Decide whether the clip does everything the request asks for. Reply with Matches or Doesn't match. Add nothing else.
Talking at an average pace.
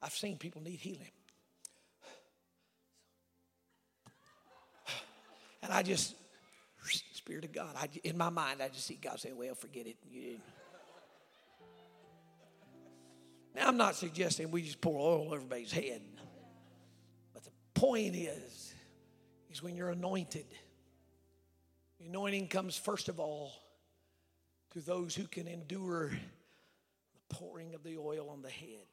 Doesn't match